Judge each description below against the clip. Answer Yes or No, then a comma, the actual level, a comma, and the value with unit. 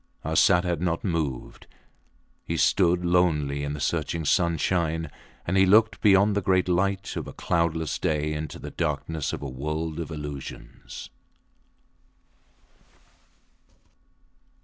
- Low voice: Yes, very low, 80 Hz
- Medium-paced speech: No, slow, 125 wpm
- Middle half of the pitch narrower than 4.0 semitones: Yes, average, 3.0 semitones